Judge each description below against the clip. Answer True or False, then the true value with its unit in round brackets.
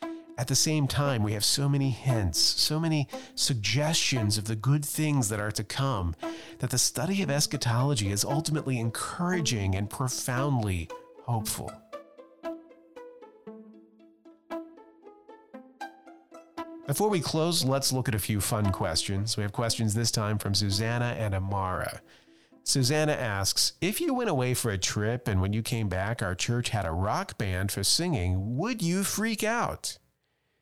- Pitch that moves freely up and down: True (8.3 semitones)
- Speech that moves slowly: False (150 wpm)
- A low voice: True (130 Hz)